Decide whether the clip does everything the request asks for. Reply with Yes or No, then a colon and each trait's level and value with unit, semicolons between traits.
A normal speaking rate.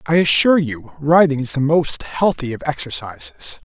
Yes: average, 160 wpm